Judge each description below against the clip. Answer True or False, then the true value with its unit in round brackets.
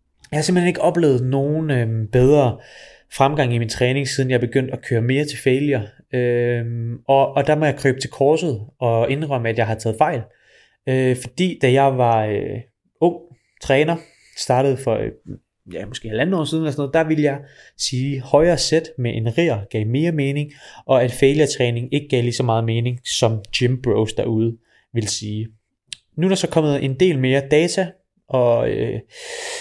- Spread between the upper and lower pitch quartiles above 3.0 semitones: True (4.0 semitones)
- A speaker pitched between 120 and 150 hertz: True (135 Hz)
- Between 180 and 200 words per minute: True (195 wpm)